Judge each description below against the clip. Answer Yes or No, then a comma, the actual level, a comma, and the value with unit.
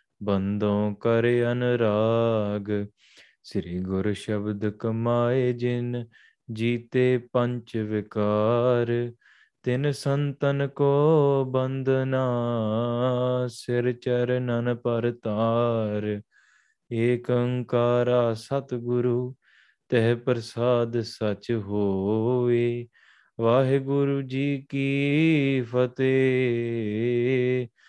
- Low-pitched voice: Yes, low, 120 Hz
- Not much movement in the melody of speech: Yes, narrow, 1.9 semitones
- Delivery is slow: Yes, slow, 65 wpm